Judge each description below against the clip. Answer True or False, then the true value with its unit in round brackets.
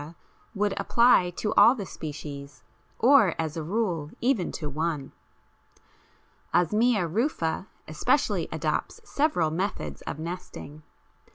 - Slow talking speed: True (110 wpm)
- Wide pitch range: True (5.9 semitones)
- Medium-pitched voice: True (175 Hz)